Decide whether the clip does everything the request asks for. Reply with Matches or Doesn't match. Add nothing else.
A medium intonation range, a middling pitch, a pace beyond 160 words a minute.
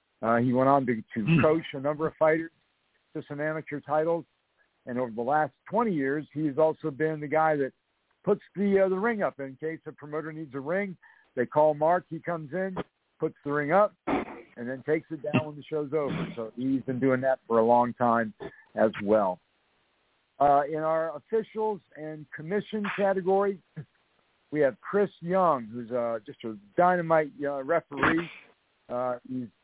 Matches